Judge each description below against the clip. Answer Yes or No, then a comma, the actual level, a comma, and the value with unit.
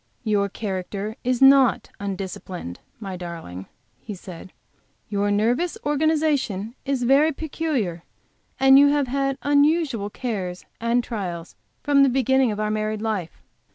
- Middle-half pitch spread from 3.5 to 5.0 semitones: No, wide, 5.6 semitones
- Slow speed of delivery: Yes, slow, 130 wpm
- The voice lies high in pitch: Yes, high, 225 Hz